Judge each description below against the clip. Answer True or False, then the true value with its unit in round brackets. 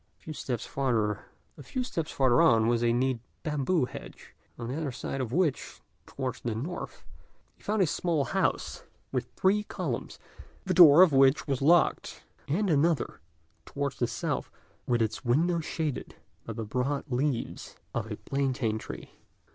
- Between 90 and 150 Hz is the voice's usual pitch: True (140 Hz)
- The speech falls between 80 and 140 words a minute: False (155 wpm)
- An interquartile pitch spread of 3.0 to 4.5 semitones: False (4.9 semitones)